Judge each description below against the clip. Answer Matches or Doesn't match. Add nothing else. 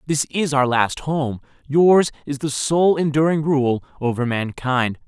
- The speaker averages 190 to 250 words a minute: Doesn't match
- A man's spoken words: Matches